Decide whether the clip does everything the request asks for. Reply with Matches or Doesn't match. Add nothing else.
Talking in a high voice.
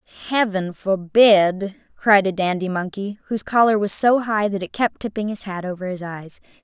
Matches